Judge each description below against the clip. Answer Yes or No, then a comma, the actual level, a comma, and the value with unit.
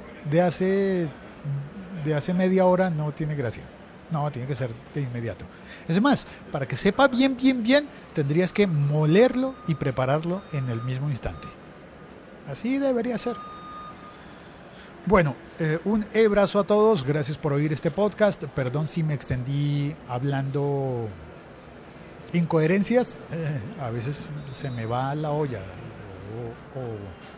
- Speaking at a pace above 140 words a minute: No, average, 130 wpm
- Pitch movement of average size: No, wide, 6.3 semitones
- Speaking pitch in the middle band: Yes, medium, 150 Hz